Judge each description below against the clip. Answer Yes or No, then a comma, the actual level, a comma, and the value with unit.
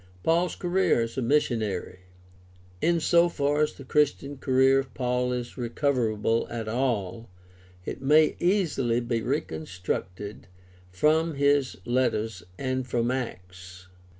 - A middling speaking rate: No, slow, 130 wpm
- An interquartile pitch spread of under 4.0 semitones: No, average, 4.4 semitones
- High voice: No, low, 125 Hz